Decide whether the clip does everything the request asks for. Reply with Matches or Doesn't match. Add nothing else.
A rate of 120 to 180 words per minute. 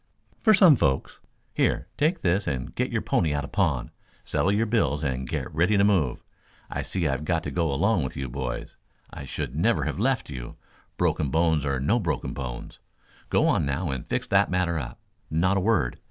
Doesn't match